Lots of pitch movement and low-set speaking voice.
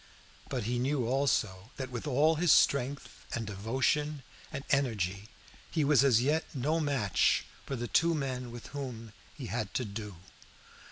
No: average, 4.0 semitones; low, 130 Hz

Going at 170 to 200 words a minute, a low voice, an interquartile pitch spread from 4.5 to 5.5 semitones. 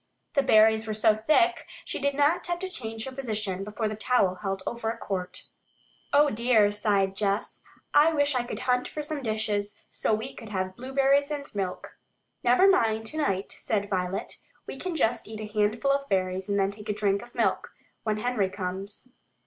No: average, 190 wpm; high, 220 Hz; average, 5.1 semitones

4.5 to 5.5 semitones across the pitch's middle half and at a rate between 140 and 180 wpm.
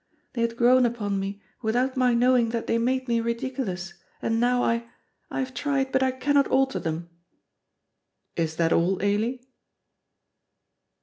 No: average, 3.9 semitones; average, 150 wpm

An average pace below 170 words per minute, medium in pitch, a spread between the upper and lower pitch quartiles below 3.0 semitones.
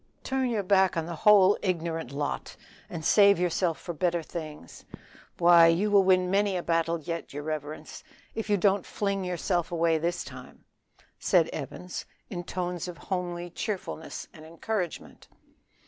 Yes: average, 155 wpm; medium, 175 Hz; narrow, 2.6 semitones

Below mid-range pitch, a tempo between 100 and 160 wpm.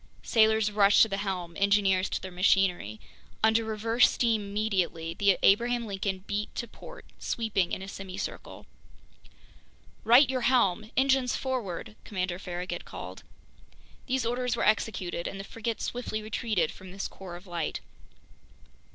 No: high, 205 Hz; average, 145 wpm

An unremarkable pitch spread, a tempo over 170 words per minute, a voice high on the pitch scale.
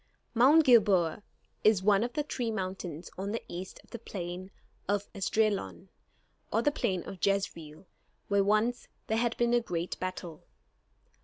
No: average, 3.9 semitones; average, 155 wpm; high, 200 Hz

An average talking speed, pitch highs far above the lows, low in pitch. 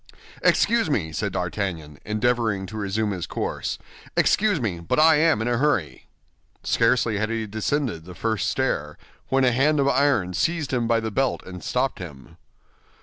Yes: average, 170 wpm; wide, 6.0 semitones; low, 110 Hz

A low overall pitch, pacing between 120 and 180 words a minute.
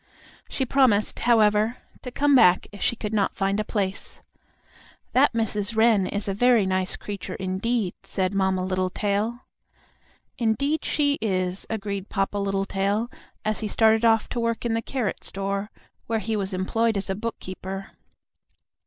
No: high, 210 Hz; average, 155 wpm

